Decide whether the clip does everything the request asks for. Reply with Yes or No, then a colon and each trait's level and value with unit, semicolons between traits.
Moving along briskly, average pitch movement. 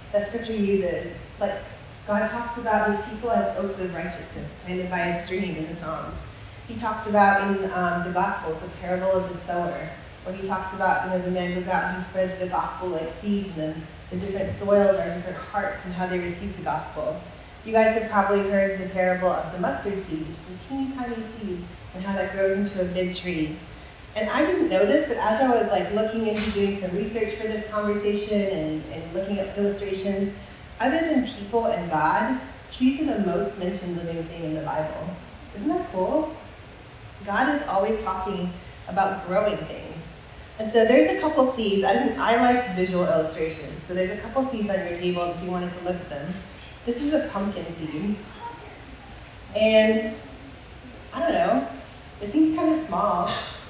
No: average, 195 wpm; average, 3.3 semitones